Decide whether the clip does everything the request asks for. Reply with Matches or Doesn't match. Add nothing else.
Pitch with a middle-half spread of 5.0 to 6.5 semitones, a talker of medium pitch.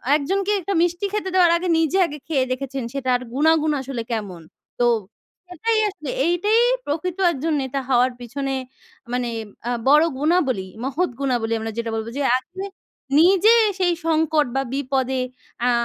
Doesn't match